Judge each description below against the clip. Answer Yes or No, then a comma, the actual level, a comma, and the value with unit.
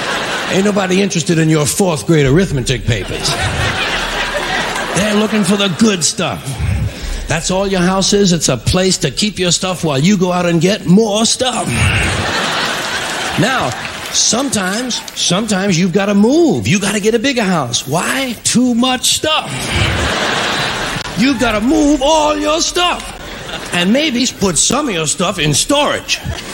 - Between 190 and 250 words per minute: No, average, 155 wpm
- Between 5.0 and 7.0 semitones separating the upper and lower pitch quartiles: Yes, wide, 5.6 semitones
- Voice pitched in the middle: No, high, 200 Hz